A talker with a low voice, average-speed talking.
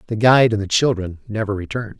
No: low, 110 Hz; fast, 210 wpm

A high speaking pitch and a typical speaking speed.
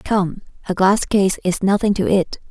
Yes: high, 195 Hz; average, 190 wpm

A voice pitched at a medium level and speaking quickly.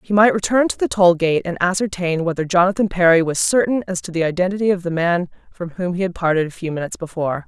Yes: medium, 180 Hz; fast, 240 wpm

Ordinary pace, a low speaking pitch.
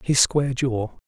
Yes: average, 165 wpm; low, 125 Hz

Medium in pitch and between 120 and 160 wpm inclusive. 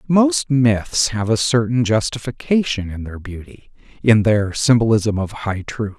No: low, 115 Hz; average, 150 wpm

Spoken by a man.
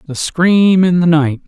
Yes: male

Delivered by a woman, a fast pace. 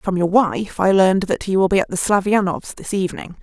Yes: female; fast, 245 wpm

